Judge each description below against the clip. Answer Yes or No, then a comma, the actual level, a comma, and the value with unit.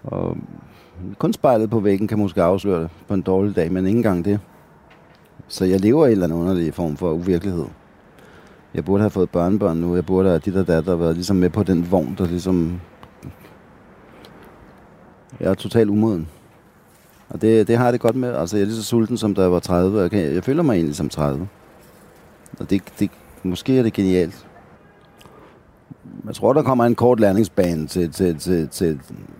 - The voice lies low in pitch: Yes, very low, 95 Hz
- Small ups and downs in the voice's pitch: No, average, 3.3 semitones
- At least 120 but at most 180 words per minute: No, average, 200 wpm